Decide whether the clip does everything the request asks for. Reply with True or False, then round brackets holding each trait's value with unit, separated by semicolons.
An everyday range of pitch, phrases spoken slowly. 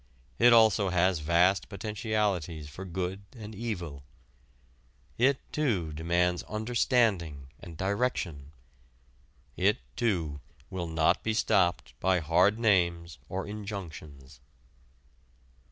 True (4.6 semitones; 100 wpm)